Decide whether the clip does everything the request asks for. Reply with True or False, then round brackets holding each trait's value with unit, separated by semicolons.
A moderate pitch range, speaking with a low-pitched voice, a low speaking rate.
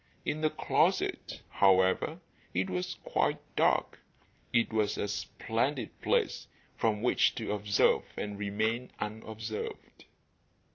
False (1.8 semitones; 105 Hz; 110 wpm)